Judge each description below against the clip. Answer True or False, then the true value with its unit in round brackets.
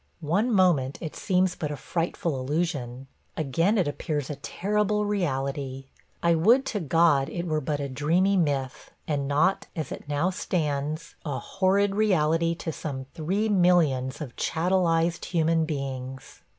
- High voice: False (160 Hz)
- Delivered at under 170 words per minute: True (150 wpm)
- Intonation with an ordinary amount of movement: True (4.3 semitones)